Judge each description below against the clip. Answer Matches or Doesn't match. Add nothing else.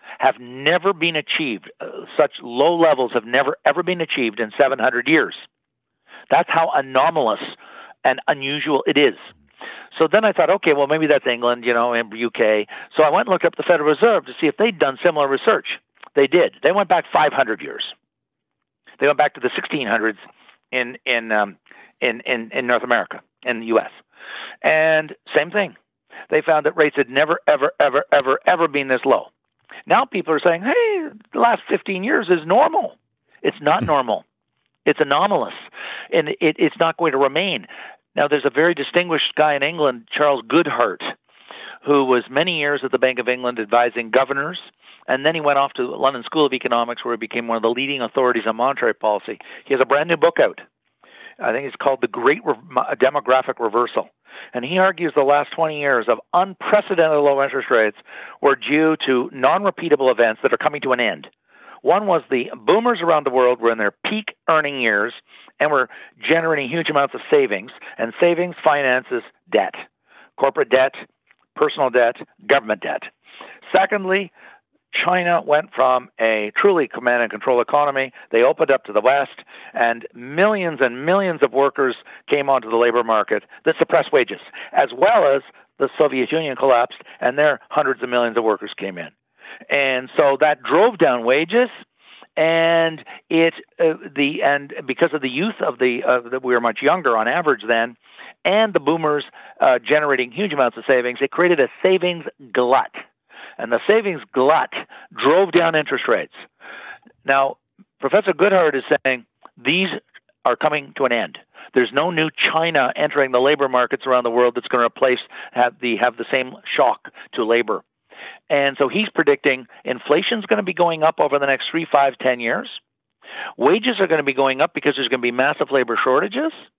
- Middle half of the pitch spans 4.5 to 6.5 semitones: Matches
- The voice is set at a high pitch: Doesn't match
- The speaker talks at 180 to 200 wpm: Matches